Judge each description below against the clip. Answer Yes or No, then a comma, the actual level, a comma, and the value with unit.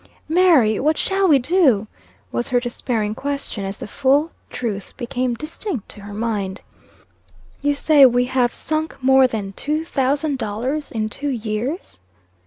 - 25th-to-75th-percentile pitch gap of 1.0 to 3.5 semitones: No, average, 5.3 semitones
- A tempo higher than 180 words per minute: No, average, 150 wpm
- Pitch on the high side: Yes, very high, 255 Hz